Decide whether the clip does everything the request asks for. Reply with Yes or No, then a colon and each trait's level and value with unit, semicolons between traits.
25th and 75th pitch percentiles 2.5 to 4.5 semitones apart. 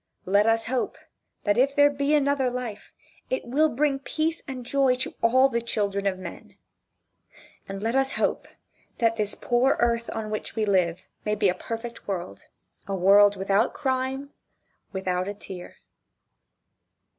No: average, 4.9 semitones